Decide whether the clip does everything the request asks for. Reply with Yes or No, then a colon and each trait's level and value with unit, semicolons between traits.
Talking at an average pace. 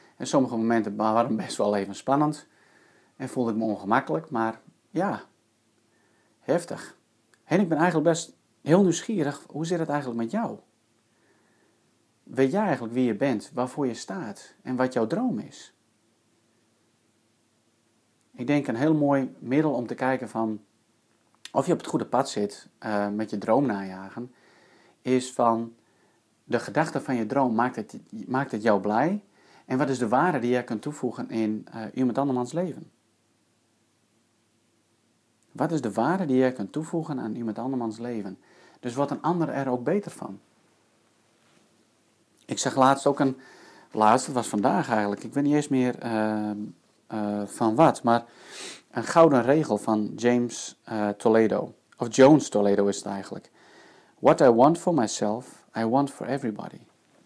Yes: average, 160 wpm